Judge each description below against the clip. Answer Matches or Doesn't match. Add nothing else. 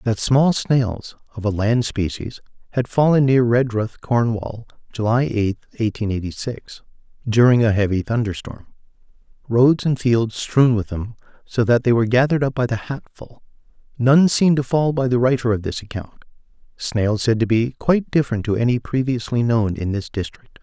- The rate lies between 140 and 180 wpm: Matches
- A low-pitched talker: Matches